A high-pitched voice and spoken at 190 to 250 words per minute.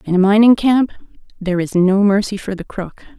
Yes: high, 200 Hz; fast, 205 wpm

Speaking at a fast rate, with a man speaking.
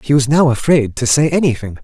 Yes: fast, 230 wpm; male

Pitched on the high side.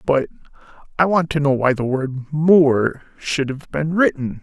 No: medium, 145 Hz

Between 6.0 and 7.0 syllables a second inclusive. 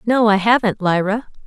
No: 4.9 syllables/s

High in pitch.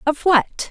Yes: very high, 300 Hz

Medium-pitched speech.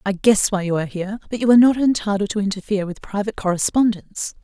No: high, 205 Hz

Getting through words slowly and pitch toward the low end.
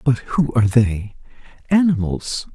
Yes: slow, 95 wpm; low, 120 Hz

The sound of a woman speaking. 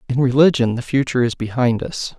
No: male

